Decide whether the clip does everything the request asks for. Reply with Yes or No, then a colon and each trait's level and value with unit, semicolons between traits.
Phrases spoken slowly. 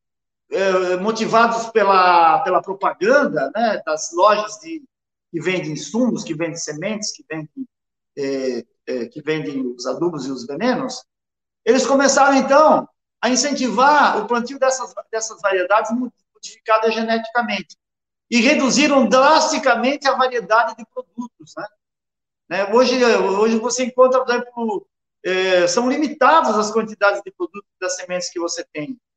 No: average, 130 wpm